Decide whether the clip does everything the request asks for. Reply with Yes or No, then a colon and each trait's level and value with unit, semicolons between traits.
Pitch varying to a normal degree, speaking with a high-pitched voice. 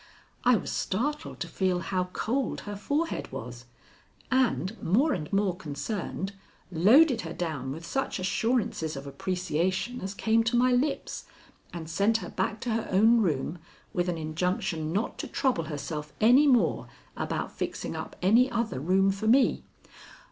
No: wide, 5.8 semitones; high, 195 Hz